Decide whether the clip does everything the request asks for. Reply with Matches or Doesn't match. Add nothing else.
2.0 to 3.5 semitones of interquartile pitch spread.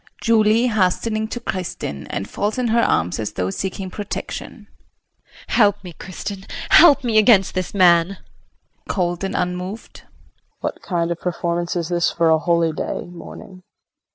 Doesn't match